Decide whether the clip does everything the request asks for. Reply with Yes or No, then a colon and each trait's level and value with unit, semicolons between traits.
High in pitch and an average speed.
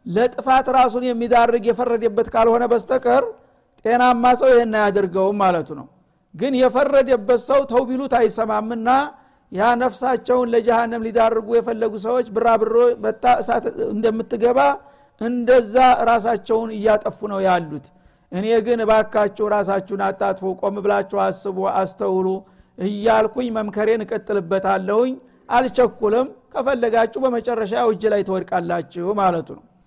Yes: high, 230 Hz; average, 100 wpm